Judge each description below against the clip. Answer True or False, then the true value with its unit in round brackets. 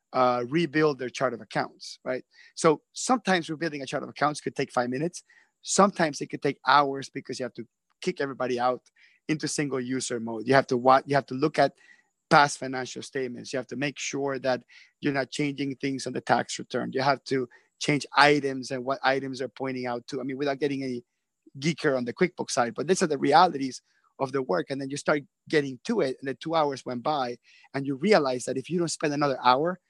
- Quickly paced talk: True (225 wpm)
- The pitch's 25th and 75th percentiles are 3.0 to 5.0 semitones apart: False (2.6 semitones)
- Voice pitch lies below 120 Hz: False (135 Hz)